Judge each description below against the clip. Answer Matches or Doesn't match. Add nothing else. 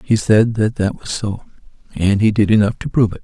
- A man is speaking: Matches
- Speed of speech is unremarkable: Doesn't match